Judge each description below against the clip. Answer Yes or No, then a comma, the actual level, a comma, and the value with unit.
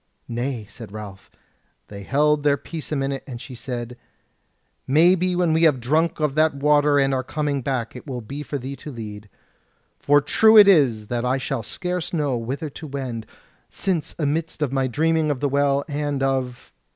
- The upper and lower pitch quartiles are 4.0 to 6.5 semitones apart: No, average, 3.4 semitones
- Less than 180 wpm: No, average, 190 wpm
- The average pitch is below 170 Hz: Yes, medium, 140 Hz